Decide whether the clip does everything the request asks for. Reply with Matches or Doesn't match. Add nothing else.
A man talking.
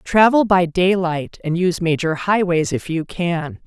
Doesn't match